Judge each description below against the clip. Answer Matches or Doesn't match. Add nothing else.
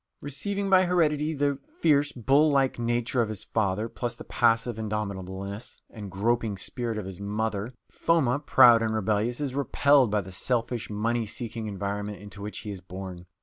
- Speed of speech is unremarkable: Matches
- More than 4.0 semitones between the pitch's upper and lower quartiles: Matches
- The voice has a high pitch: Doesn't match